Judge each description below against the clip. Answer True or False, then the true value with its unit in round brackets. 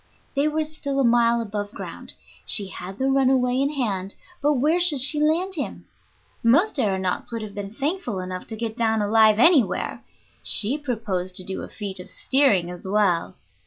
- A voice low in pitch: False (230 Hz)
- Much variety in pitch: True (5.7 semitones)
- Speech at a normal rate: True (180 wpm)